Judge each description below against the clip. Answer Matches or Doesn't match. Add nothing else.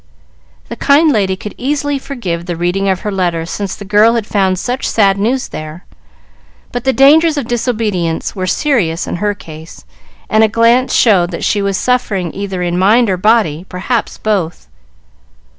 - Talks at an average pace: Matches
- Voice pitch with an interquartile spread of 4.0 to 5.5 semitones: Matches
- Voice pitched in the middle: Doesn't match